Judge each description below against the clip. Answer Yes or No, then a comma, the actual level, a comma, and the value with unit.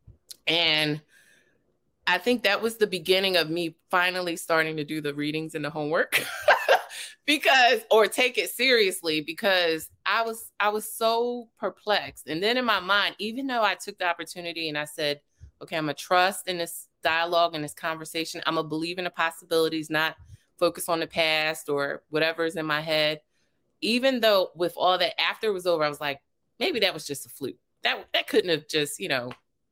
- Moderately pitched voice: Yes, medium, 170 Hz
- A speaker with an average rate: Yes, average, 190 wpm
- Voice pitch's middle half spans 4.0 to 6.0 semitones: Yes, average, 4.4 semitones